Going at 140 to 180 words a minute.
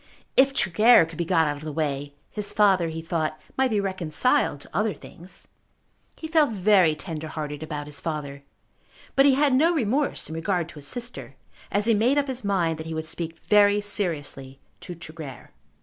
No: average, 195 wpm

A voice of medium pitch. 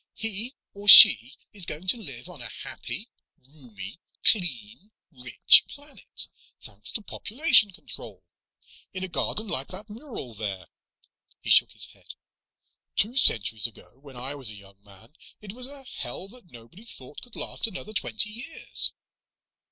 Yes: medium, 165 Hz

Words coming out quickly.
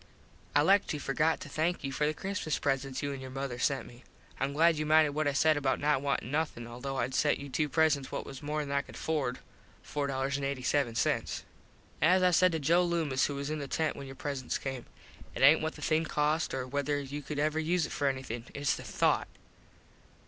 Yes: fast, 220 wpm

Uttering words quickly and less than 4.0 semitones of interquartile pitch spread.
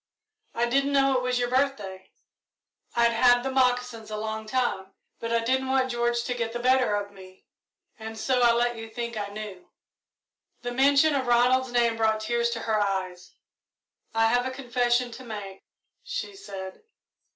No: average, 175 wpm; average, 2.7 semitones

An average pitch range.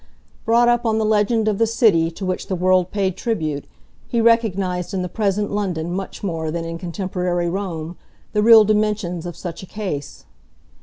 Yes: average, 3.6 semitones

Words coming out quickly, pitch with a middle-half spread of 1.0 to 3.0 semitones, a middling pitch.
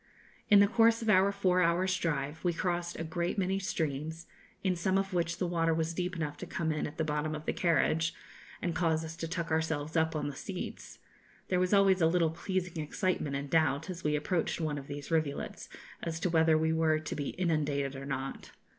Yes: fast, 215 wpm; average, 2.7 semitones; medium, 165 Hz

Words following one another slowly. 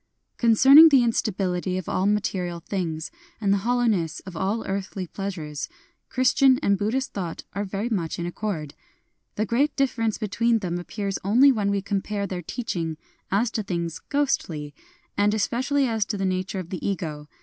No: average, 175 wpm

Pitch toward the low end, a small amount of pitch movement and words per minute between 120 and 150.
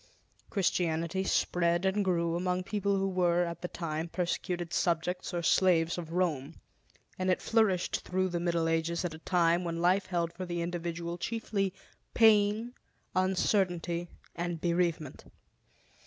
No: medium, 175 Hz; narrow, 1.8 semitones; average, 140 wpm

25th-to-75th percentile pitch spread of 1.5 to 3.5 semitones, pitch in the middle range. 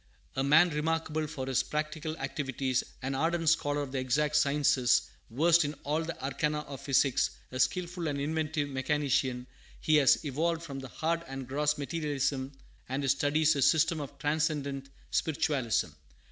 Yes: average, 2.7 semitones; medium, 145 Hz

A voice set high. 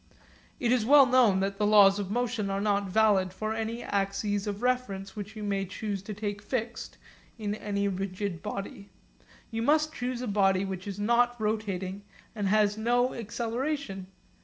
Yes: high, 210 Hz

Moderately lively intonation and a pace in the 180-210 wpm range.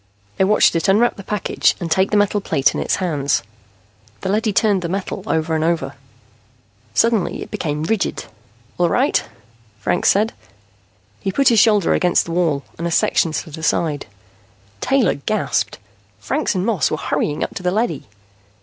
No: average, 4.6 semitones; average, 170 wpm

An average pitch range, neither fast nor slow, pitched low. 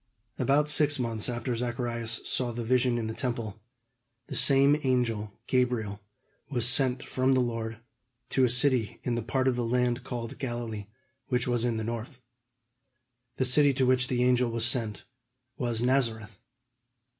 No: narrow, 1.9 semitones; average, 160 wpm; low, 120 Hz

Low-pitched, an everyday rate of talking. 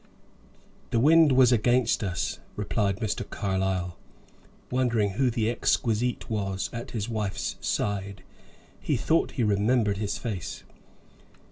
No: low, 110 Hz; slow, 120 wpm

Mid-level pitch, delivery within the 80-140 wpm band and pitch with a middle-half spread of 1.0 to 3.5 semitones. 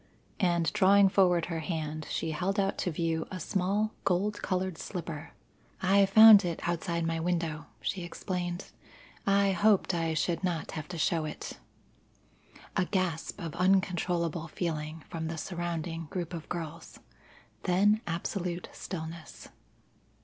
Yes: medium, 175 Hz; slow, 135 wpm; narrow, 2.5 semitones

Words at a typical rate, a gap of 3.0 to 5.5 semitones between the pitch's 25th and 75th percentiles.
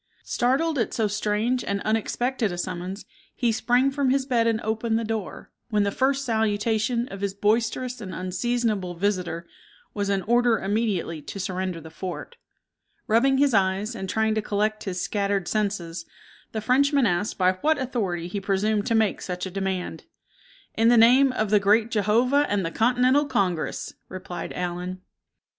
Yes: average, 165 wpm; average, 4.0 semitones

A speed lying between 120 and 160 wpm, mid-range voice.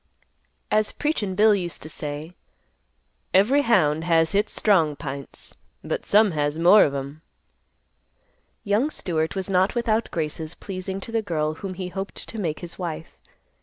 Yes: average, 155 wpm; medium, 180 Hz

